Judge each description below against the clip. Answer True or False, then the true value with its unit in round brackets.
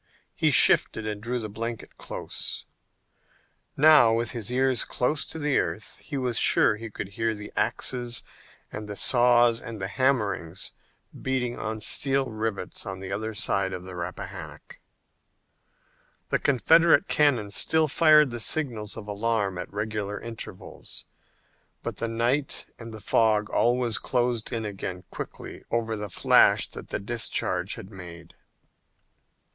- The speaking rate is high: False (145 wpm)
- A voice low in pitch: True (115 Hz)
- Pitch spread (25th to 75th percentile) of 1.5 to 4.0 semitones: True (3.3 semitones)